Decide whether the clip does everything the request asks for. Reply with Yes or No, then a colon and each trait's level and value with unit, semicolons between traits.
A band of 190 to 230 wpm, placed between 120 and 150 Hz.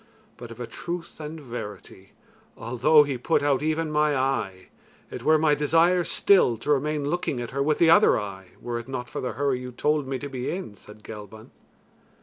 Yes: average, 200 wpm; low, 135 Hz